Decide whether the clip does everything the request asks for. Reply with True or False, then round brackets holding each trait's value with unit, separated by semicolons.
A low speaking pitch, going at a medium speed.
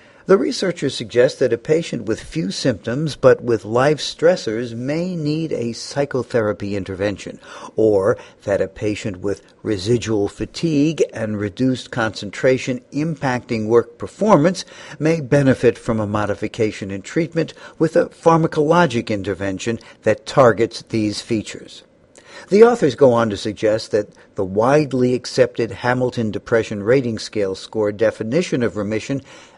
False (120 Hz; 130 wpm)